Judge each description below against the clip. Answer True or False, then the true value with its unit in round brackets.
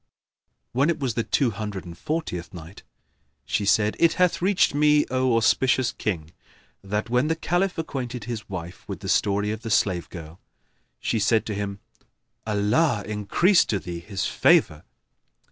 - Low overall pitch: True (110 Hz)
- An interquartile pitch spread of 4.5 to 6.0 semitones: True (5.5 semitones)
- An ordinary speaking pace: True (160 wpm)